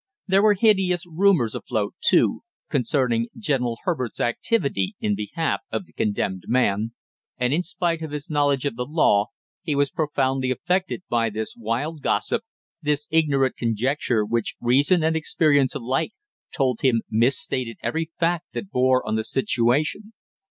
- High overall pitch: No, low, 135 Hz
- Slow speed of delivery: No, average, 150 wpm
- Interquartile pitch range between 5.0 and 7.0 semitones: Yes, wide, 5.6 semitones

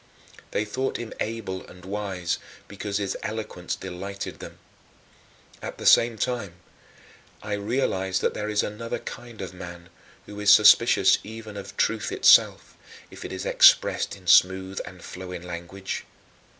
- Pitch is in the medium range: No, low, 100 Hz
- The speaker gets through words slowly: No, average, 145 wpm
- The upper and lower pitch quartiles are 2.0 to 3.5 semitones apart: Yes, narrow, 2.5 semitones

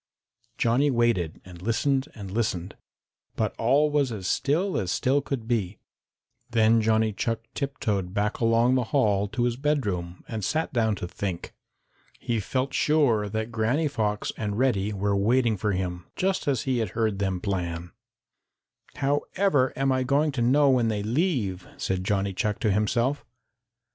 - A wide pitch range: No, average, 4.8 semitones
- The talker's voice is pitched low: Yes, low, 115 Hz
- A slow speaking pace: No, average, 160 wpm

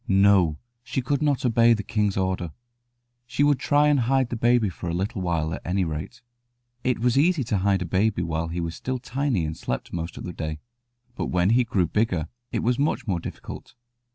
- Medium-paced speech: No, fast, 210 wpm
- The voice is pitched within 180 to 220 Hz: No, low, 100 Hz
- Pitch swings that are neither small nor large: No, wide, 6.0 semitones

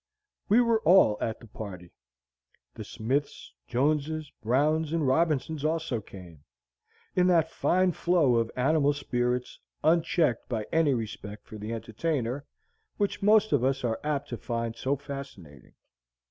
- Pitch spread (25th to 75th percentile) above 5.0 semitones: Yes, wide, 5.6 semitones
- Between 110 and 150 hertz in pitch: Yes, medium, 140 Hz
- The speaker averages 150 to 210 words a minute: No, average, 140 wpm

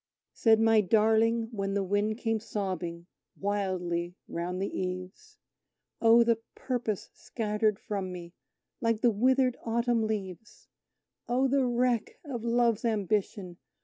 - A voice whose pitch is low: No, high, 215 Hz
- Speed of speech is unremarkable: No, slow, 125 wpm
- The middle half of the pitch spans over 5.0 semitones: No, average, 3.4 semitones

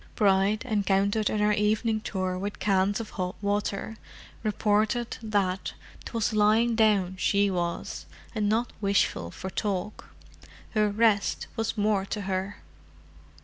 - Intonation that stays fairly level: Yes, narrow, 1.9 semitones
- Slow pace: Yes, slow, 130 wpm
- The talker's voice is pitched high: Yes, high, 205 Hz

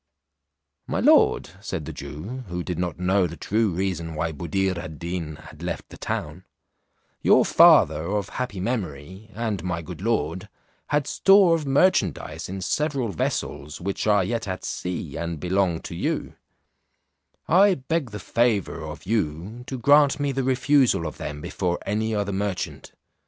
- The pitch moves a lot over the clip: Yes, wide, 6.1 semitones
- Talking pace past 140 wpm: Yes, average, 160 wpm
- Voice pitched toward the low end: Yes, very low, 95 Hz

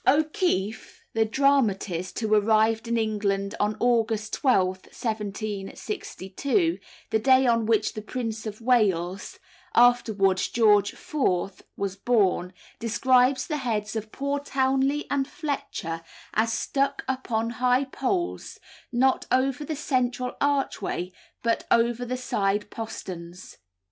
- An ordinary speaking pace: No, slow, 120 wpm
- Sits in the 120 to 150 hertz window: No, high, 230 Hz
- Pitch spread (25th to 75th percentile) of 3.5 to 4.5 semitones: Yes, average, 4.1 semitones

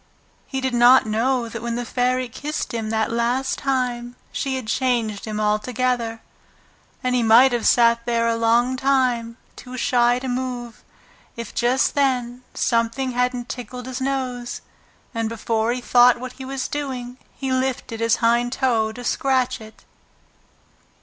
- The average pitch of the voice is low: No, high, 245 Hz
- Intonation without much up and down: Yes, narrow, 1.8 semitones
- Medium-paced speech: Yes, average, 155 wpm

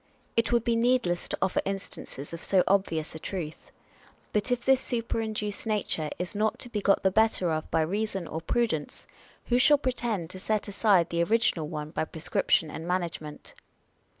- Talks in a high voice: Yes, high, 195 Hz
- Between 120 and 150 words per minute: No, average, 180 wpm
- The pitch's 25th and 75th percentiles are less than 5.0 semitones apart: No, wide, 5.4 semitones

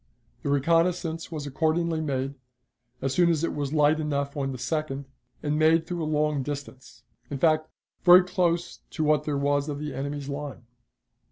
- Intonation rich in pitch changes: No, narrow, 2.4 semitones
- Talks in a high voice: No, medium, 150 Hz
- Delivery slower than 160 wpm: No, average, 175 wpm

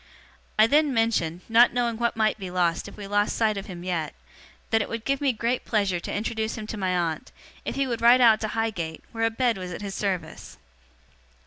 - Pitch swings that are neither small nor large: Yes, average, 3.8 semitones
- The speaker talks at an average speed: No, fast, 225 wpm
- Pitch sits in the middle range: No, high, 220 Hz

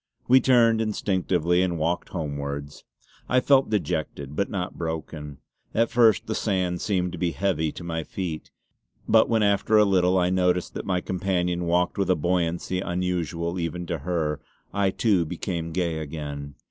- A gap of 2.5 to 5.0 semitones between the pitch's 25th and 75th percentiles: Yes, average, 3.0 semitones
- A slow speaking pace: No, average, 165 wpm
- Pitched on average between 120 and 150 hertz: No, very low, 90 Hz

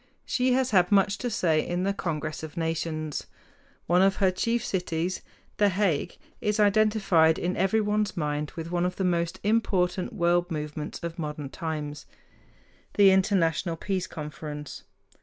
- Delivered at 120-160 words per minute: Yes, average, 150 wpm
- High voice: No, medium, 180 Hz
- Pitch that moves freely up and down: No, average, 3.7 semitones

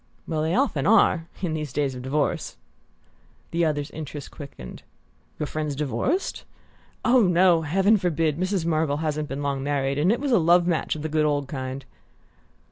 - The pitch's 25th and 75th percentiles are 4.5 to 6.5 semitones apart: No, average, 3.5 semitones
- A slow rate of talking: No, average, 175 wpm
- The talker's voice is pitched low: No, medium, 155 Hz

